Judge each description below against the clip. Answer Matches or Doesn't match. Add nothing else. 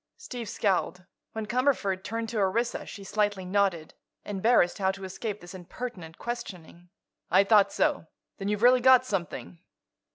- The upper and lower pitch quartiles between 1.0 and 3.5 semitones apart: Doesn't match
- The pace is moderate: Matches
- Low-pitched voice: Doesn't match